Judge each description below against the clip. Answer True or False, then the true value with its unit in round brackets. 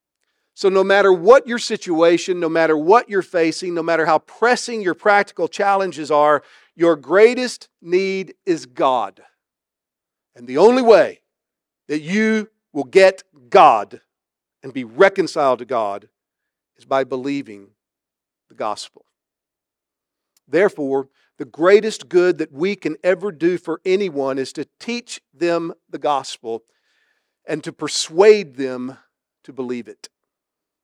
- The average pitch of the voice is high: False (175 Hz)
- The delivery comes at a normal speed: False (130 wpm)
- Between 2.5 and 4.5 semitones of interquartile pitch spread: False (5.1 semitones)